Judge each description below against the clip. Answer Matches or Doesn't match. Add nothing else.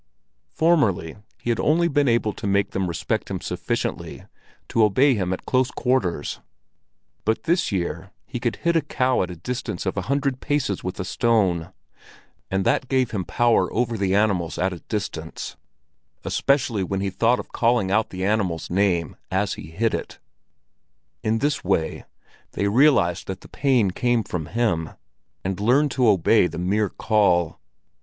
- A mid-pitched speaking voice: Doesn't match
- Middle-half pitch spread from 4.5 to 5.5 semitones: Matches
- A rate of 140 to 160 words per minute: Doesn't match